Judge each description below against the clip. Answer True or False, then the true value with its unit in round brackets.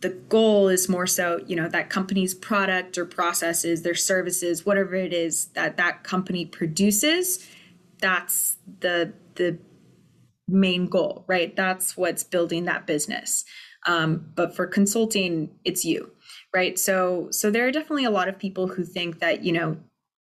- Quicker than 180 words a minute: False (155 wpm)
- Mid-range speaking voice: True (180 Hz)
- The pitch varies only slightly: True (1.9 semitones)